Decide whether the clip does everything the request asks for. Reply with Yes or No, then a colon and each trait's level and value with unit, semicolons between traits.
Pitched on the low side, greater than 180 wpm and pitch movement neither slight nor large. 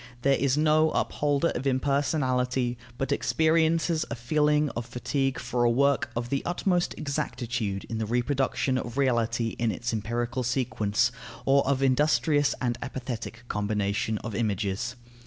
No: low, 125 Hz; average, 140 wpm; average, 3.3 semitones